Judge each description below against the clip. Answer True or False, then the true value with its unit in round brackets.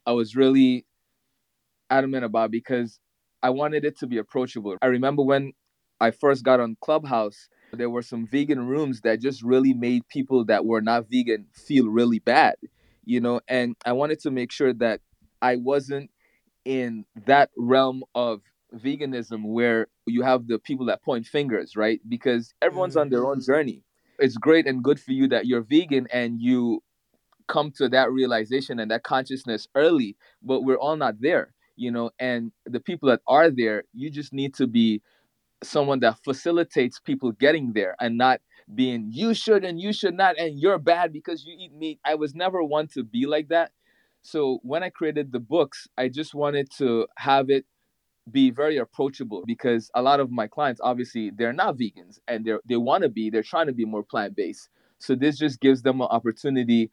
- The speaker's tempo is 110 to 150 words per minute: False (190 wpm)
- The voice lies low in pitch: True (130 Hz)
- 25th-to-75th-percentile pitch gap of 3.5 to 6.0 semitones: True (3.9 semitones)